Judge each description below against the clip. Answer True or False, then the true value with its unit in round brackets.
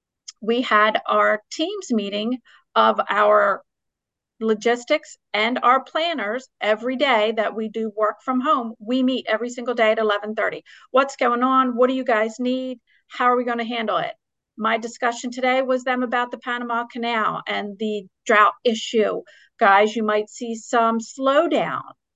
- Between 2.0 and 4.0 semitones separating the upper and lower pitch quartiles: True (2.8 semitones)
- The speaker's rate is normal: True (165 wpm)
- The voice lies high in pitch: True (235 Hz)